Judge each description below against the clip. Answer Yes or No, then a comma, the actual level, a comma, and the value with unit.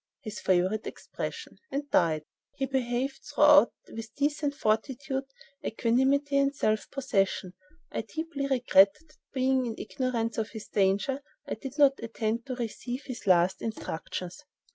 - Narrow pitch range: No, average, 4.3 semitones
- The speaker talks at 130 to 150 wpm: Yes, average, 140 wpm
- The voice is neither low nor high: No, very high, 250 Hz